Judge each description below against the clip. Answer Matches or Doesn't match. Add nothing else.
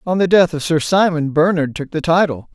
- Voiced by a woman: Doesn't match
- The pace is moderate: Doesn't match